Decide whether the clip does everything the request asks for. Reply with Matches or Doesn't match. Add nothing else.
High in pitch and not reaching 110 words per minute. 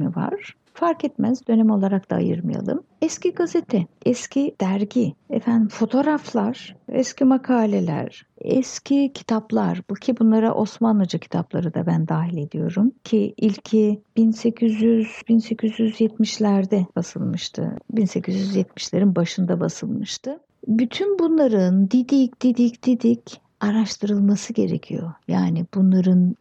Matches